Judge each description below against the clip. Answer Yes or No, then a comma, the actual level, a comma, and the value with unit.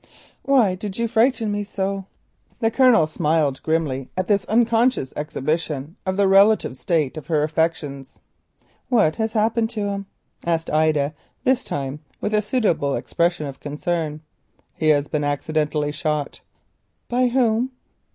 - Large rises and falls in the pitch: Yes, wide, 6.5 semitones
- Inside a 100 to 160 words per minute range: Yes, average, 140 wpm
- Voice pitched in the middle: Yes, medium, 170 Hz